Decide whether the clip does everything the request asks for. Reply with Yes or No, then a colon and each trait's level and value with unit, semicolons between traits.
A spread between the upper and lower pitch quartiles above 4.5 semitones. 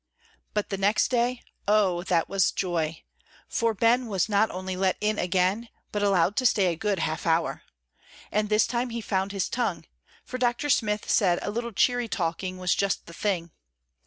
No: average, 3.7 semitones